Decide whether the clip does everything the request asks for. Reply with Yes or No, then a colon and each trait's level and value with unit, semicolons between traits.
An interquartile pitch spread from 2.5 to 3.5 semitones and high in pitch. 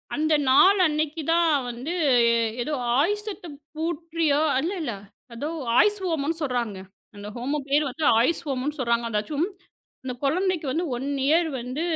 No: average, 4.5 semitones; very high, 300 Hz